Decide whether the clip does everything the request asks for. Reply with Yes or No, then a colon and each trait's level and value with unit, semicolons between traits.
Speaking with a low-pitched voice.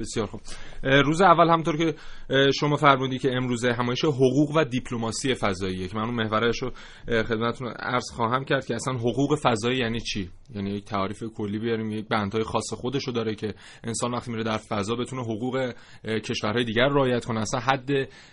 Yes: low, 120 Hz